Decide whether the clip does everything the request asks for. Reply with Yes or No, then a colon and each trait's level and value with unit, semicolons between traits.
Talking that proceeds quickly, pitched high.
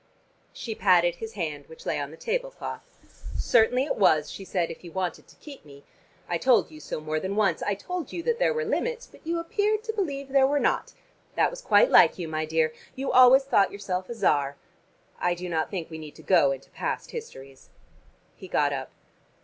Yes: fast, 215 wpm; high, 195 Hz